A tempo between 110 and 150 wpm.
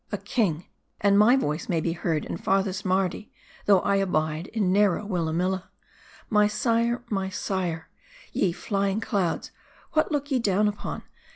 No: average, 160 wpm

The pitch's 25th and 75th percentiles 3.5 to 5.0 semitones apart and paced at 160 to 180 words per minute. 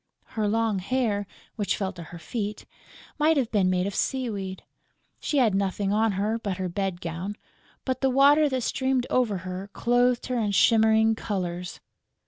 Yes: average, 4.4 semitones; average, 170 wpm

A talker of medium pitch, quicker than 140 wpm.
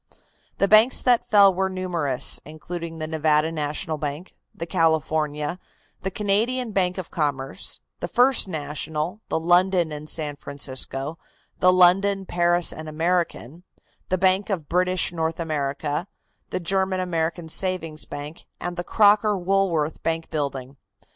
No: medium, 170 Hz; slow, 135 wpm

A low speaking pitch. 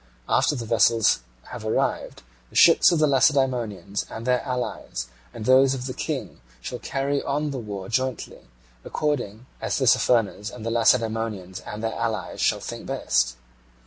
Yes: low, 115 Hz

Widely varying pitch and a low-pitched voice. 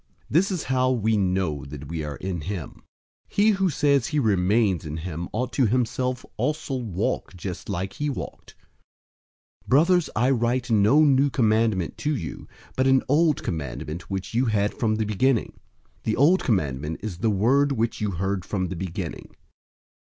Yes: wide, 6.3 semitones; low, 110 Hz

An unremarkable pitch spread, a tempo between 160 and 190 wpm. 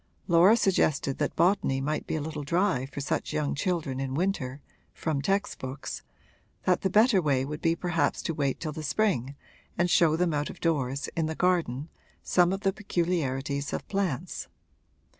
Yes: average, 4.4 semitones; average, 180 wpm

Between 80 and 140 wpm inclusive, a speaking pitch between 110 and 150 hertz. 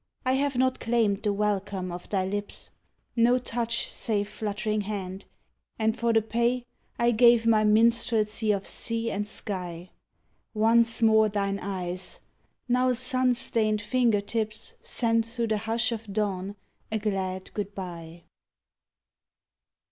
No: slow, 135 wpm; high, 215 Hz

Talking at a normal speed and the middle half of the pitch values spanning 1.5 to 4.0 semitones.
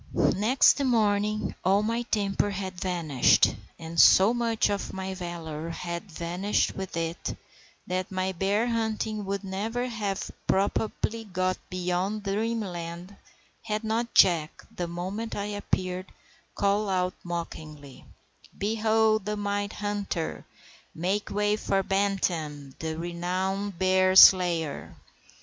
No: slow, 120 wpm; average, 3.1 semitones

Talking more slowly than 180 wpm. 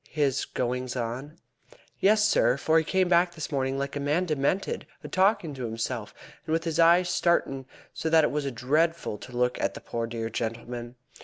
No: average, 190 wpm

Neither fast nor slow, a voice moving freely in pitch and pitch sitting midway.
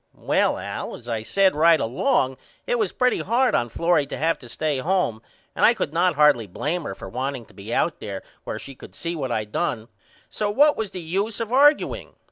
No: fast, 220 wpm; wide, 8.6 semitones; medium, 160 Hz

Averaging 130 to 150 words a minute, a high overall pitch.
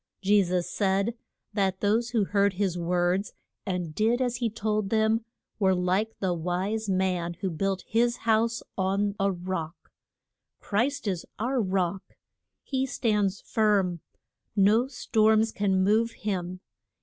Yes: slow, 135 wpm; high, 200 Hz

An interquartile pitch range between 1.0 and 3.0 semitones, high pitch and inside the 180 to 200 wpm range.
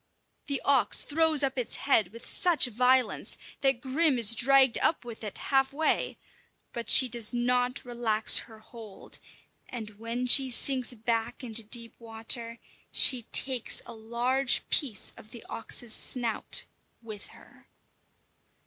No: average, 2.7 semitones; high, 240 Hz; average, 140 wpm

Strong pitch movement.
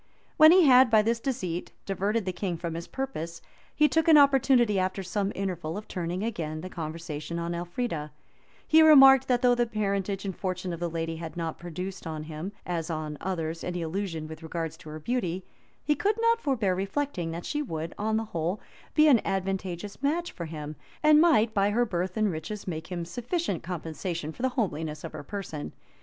Yes: wide, 6.0 semitones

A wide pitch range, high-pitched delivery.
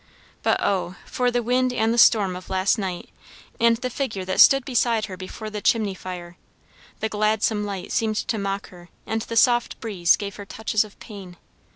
No: average, 3.3 semitones; high, 210 Hz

